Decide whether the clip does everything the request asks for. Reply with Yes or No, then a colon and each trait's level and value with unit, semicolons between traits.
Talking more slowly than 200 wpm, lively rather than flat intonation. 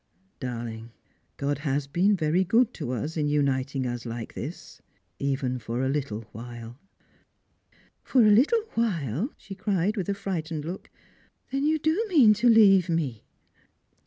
Yes: average, 160 wpm; wide, 8.2 semitones